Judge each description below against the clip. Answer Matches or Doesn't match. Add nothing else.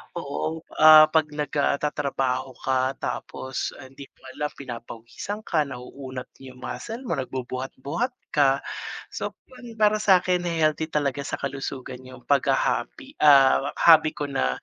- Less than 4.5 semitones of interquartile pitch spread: Matches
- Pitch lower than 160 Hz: Matches